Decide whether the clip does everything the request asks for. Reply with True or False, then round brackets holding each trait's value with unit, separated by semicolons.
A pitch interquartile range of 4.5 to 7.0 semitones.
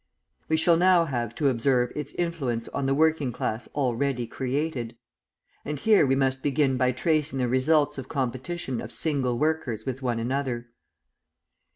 False (3.6 semitones)